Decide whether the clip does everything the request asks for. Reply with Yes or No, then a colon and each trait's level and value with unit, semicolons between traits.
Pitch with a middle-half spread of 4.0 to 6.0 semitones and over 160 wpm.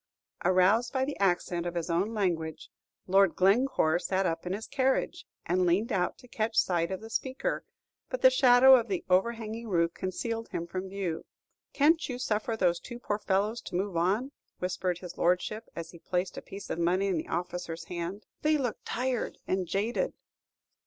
Yes: average, 4.8 semitones; average, 185 wpm